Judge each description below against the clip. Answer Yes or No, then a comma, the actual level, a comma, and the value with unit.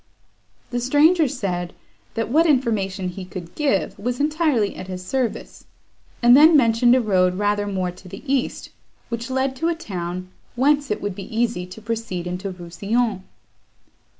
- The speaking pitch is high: Yes, high, 220 Hz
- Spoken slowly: No, average, 160 wpm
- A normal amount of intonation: No, wide, 6.0 semitones